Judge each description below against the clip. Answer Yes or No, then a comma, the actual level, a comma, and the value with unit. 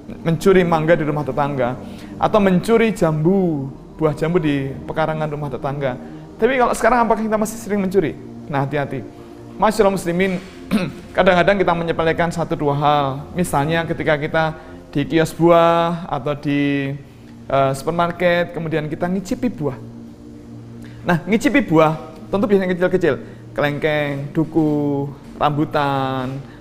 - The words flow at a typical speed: Yes, average, 120 wpm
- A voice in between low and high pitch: Yes, medium, 155 Hz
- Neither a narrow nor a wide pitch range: Yes, average, 3.9 semitones